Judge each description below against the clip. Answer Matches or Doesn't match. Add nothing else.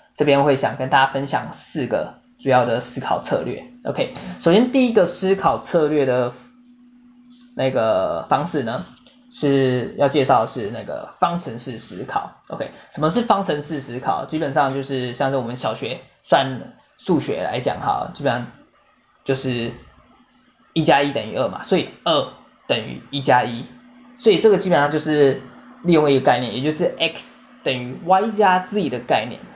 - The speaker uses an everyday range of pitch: Doesn't match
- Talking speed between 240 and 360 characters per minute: Matches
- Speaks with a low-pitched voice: Doesn't match